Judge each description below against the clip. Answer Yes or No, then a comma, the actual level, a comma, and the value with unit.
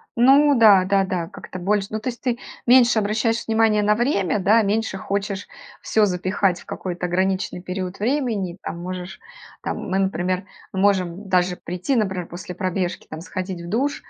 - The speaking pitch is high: Yes, high, 195 Hz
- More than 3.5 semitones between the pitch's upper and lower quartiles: No, average, 3.2 semitones